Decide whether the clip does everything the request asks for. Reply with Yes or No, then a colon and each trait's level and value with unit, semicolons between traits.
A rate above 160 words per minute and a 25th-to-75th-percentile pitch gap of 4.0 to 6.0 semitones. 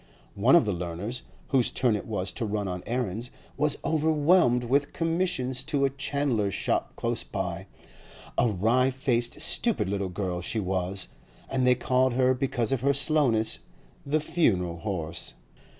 No: average, 155 wpm; wide, 5.4 semitones